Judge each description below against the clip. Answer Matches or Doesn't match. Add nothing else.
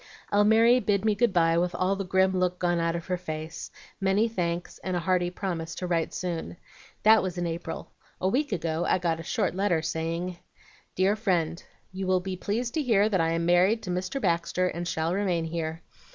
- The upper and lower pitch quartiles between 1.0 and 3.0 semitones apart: Matches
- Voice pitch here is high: Doesn't match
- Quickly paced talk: Matches